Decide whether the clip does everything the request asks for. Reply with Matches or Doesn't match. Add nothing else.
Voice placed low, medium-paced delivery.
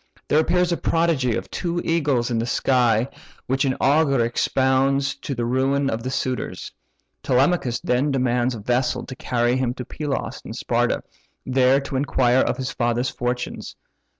Matches